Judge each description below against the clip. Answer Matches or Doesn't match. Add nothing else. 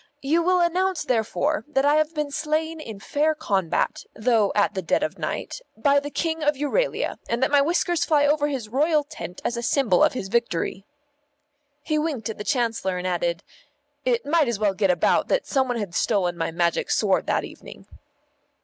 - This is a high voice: Matches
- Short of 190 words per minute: Doesn't match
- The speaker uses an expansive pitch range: Matches